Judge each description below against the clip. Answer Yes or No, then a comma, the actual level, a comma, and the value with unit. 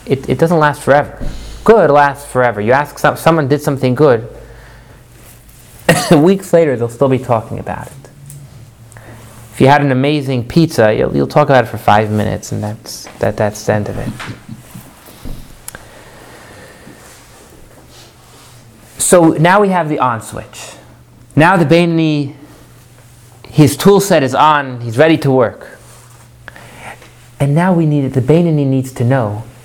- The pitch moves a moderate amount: Yes, average, 4.1 semitones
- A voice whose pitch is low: Yes, low, 130 Hz